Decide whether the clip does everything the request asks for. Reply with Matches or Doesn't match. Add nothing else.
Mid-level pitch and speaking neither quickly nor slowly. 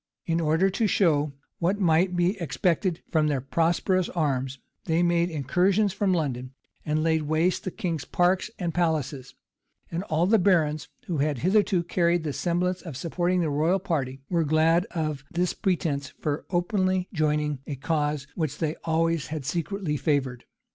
Matches